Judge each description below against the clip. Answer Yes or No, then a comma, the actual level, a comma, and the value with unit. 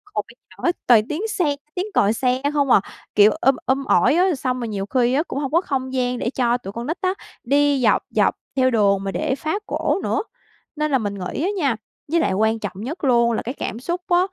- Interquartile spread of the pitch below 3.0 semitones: No, average, 4.8 semitones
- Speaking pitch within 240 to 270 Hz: Yes, very high, 260 Hz